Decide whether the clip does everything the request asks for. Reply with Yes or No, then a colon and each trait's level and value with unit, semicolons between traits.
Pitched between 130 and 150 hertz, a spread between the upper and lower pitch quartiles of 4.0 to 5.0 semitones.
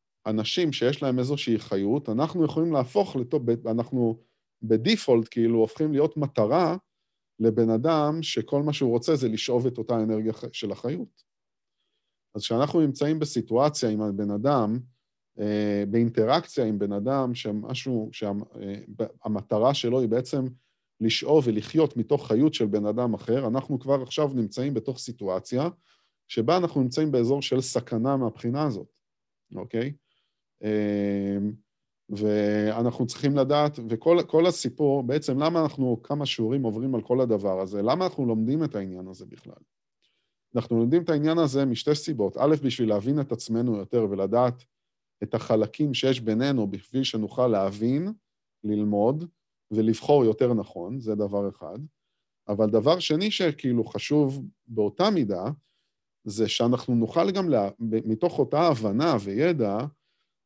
No: low, 120 Hz; average, 4.7 semitones